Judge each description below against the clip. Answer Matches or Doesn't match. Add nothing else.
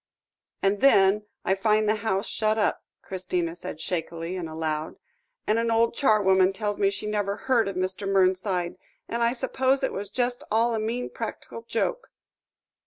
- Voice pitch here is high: Matches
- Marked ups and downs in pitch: Doesn't match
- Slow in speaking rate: Doesn't match